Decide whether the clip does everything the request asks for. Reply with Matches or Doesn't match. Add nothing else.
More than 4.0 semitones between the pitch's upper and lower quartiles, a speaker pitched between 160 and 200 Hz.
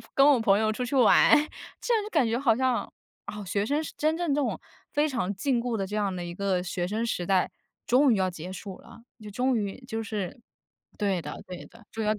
Doesn't match